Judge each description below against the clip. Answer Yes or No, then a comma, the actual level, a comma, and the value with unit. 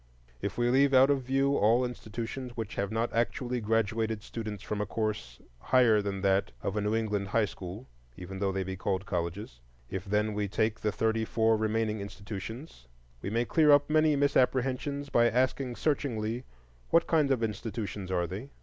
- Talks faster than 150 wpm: Yes, average, 180 wpm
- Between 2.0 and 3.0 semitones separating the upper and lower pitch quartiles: No, average, 3.8 semitones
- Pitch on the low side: Yes, low, 110 Hz